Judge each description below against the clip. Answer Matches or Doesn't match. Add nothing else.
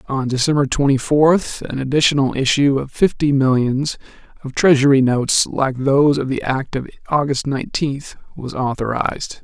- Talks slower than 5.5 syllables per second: Matches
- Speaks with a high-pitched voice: Doesn't match